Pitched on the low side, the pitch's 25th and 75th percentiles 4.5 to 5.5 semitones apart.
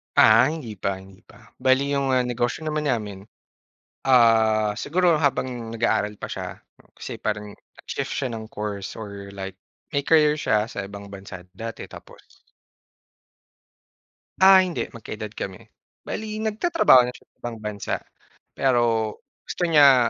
Yes: low, 115 Hz; average, 5.1 semitones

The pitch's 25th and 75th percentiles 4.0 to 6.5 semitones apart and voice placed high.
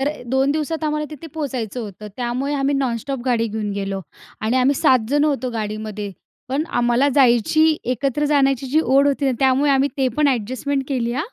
No: average, 3.4 semitones; very high, 265 Hz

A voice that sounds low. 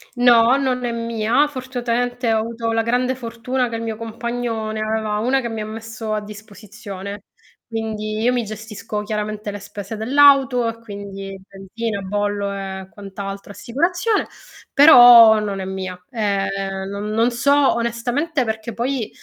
No: high, 225 Hz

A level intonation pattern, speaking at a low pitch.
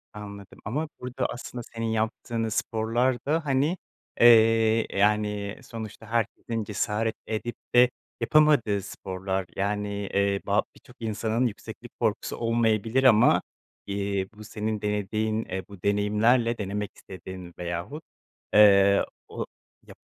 Yes: narrow, 2.3 semitones; low, 110 Hz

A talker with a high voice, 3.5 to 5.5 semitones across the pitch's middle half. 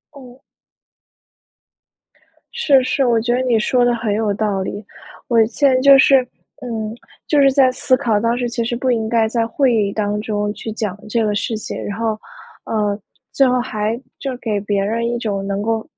No: high, 230 Hz; average, 2.9 semitones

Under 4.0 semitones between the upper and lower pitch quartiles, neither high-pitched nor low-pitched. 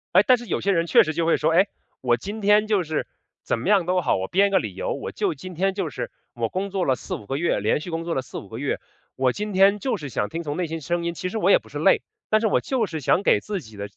No: average, 4.9 semitones; medium, 180 Hz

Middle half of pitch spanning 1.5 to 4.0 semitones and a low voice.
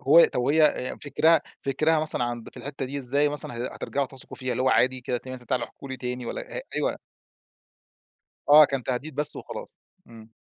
Yes: average, 2.8 semitones; low, 130 Hz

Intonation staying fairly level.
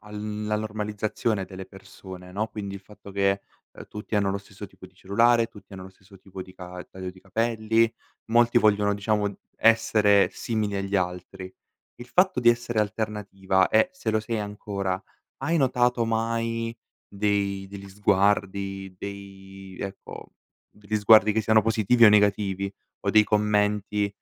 Yes: narrow, 2.1 semitones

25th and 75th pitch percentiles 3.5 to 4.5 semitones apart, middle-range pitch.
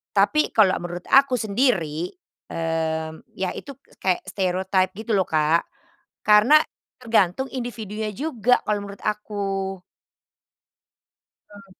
No: average, 3.8 semitones; high, 200 Hz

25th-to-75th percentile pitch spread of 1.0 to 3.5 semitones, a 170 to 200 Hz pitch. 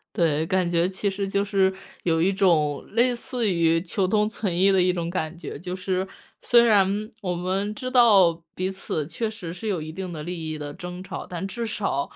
Yes: average, 3.0 semitones; medium, 185 Hz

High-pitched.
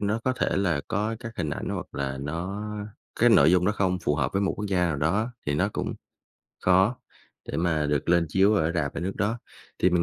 No: very low, 90 Hz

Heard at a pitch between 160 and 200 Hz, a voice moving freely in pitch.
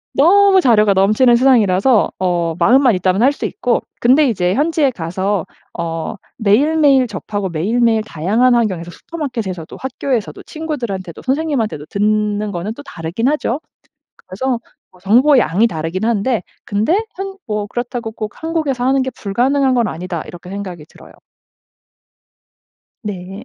No: high, 220 Hz; wide, 5.8 semitones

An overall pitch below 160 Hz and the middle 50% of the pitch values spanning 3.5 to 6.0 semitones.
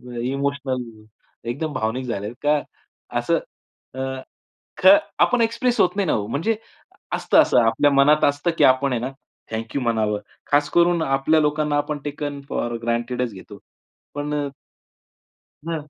Yes: medium, 140 Hz; average, 3.9 semitones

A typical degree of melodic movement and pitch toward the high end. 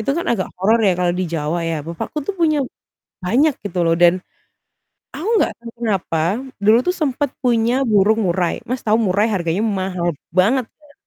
No: wide, 5.9 semitones; high, 210 Hz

